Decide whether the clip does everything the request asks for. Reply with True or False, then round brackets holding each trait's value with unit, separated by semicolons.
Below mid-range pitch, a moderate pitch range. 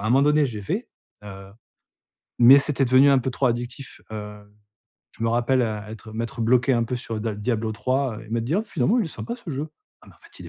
True (120 Hz; 3.6 semitones)